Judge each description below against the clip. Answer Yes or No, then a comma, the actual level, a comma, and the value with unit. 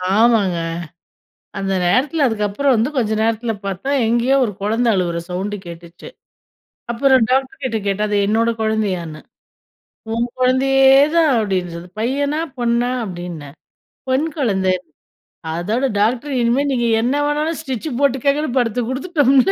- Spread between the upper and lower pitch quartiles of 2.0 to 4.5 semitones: No, average, 4.9 semitones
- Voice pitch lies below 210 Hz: No, high, 235 Hz